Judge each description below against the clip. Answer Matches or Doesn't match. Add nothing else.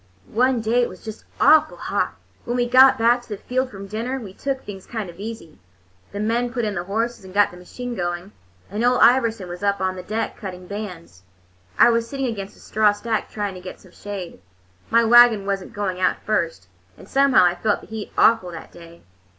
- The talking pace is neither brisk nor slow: Doesn't match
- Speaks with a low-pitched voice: Doesn't match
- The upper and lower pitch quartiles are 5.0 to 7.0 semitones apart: Doesn't match